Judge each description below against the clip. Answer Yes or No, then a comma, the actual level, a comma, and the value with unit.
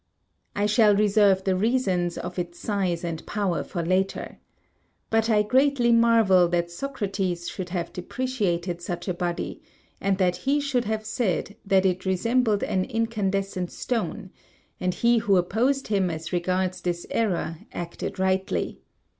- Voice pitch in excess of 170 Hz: Yes, high, 190 Hz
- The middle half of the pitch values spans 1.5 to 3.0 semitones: No, average, 3.8 semitones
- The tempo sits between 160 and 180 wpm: No, average, 145 wpm